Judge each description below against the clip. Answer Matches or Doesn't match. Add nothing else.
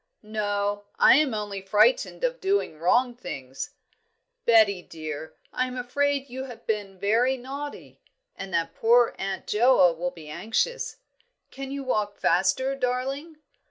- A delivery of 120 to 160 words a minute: Matches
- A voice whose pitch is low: Doesn't match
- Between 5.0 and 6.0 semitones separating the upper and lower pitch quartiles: Matches